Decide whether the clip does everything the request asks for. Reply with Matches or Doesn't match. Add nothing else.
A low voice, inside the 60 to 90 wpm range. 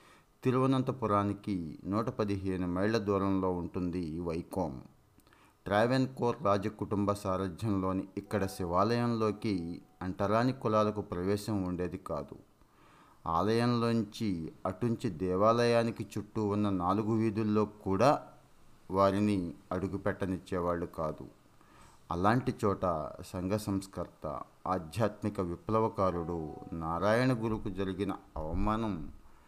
Matches